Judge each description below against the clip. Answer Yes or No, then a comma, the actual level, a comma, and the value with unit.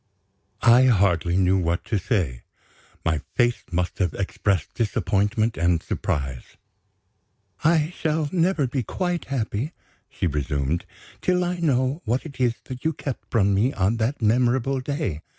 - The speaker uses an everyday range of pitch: No, wide, 7.2 semitones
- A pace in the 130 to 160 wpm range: Yes, average, 145 wpm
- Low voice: Yes, low, 115 Hz